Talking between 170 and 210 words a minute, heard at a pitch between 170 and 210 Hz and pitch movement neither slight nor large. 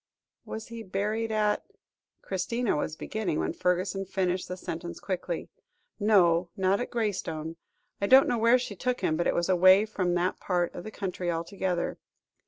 Yes: average, 175 wpm; high, 190 Hz; average, 3.5 semitones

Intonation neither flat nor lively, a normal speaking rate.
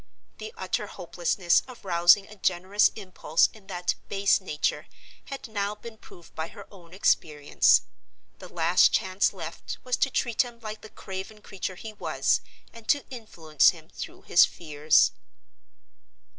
Yes: average, 3.9 semitones; average, 150 wpm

